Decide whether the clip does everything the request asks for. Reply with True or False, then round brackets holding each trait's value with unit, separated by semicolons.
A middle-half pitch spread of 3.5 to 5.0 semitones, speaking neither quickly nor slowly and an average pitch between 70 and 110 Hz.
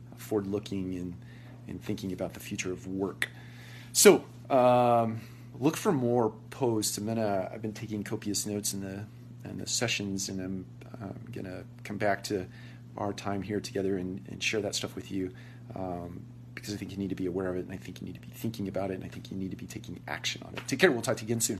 False (3.9 semitones; 235 wpm; 105 Hz)